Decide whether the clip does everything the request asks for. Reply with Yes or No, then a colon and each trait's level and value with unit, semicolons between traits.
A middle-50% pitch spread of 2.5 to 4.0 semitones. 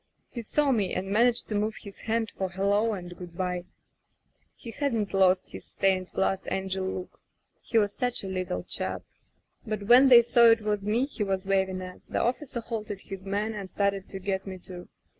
Yes: average, 3.1 semitones